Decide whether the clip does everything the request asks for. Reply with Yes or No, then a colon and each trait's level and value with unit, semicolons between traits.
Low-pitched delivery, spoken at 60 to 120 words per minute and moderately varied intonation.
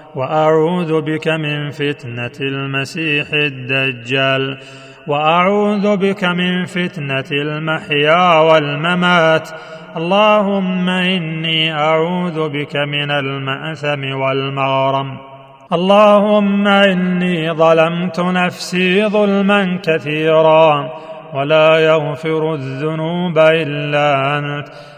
No: medium, 160 Hz; average, 70 wpm; average, 3.5 semitones